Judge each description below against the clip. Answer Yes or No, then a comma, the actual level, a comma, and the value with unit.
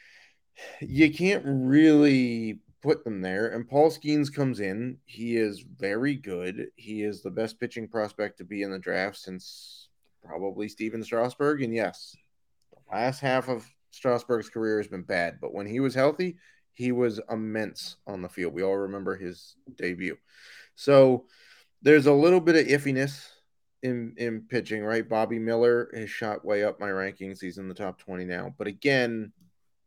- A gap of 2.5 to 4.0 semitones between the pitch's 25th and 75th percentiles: No, average, 4.8 semitones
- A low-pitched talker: Yes, low, 115 Hz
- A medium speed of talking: Yes, average, 170 wpm